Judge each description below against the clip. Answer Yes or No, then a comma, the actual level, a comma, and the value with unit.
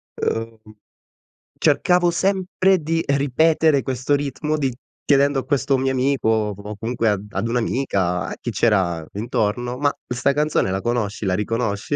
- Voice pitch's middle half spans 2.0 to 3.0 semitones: No, average, 5.2 semitones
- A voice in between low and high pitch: No, low, 125 Hz